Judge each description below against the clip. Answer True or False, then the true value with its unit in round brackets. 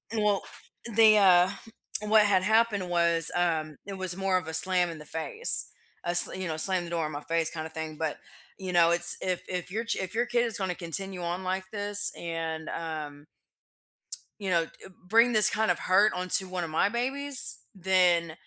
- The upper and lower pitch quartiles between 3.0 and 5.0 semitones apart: True (3.5 semitones)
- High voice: False (180 Hz)